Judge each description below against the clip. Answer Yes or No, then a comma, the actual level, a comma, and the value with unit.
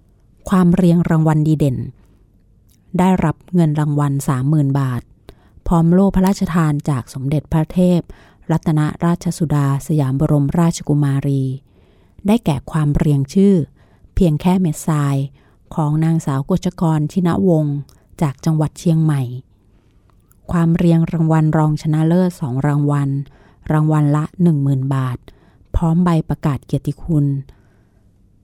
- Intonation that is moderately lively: Yes, average, 3.7 semitones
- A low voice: No, medium, 150 Hz